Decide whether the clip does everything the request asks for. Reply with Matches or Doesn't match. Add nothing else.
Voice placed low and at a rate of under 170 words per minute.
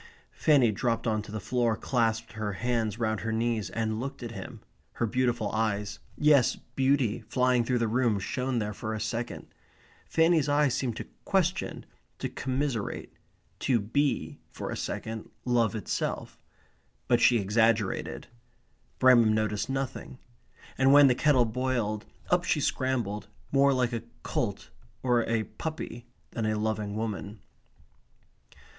Matches